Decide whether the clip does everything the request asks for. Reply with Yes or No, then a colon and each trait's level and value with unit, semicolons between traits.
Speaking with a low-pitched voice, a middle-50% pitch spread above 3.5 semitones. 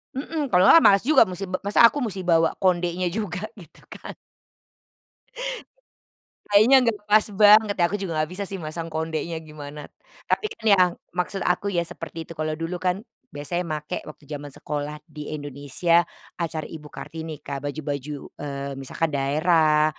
No: medium, 170 Hz; average, 4.4 semitones